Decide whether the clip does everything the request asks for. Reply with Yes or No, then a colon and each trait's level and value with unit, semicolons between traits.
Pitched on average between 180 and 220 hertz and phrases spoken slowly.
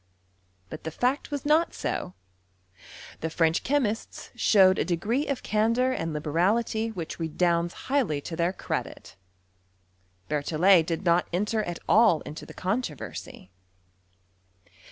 Yes: medium, 185 Hz; slow, 130 wpm